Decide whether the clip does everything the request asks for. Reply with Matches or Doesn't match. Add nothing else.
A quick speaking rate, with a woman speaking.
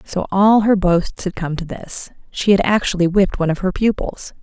Matches